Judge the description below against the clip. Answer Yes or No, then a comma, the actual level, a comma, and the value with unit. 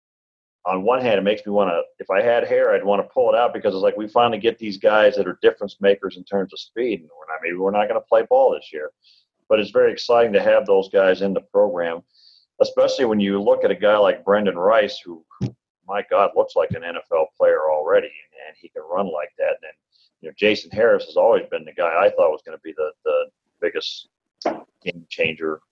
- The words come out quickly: Yes, fast, 235 wpm